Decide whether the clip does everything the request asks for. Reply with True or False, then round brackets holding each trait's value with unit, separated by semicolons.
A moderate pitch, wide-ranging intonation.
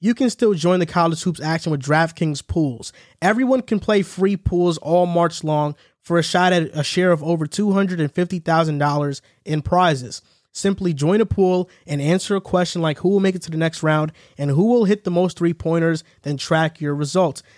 False (170 Hz; 3.1 semitones)